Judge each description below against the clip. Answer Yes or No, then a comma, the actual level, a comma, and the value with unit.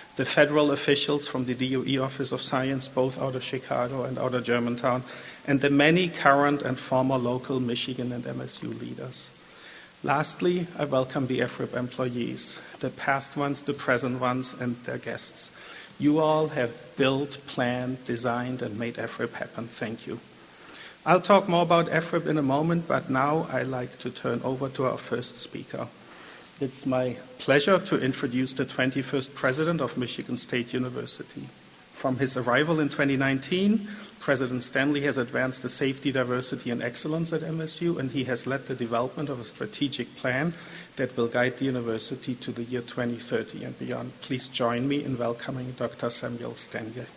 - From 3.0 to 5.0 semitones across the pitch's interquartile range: No, narrow, 2.5 semitones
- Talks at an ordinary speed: Yes, average, 165 wpm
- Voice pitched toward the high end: No, low, 130 Hz